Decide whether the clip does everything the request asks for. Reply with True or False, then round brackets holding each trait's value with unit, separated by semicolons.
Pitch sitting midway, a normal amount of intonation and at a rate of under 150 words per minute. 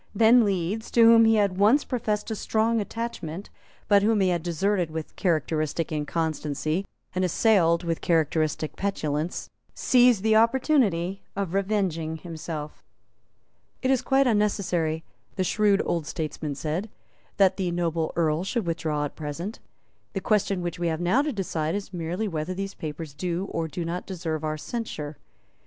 False (180 Hz; 4.6 semitones; 155 wpm)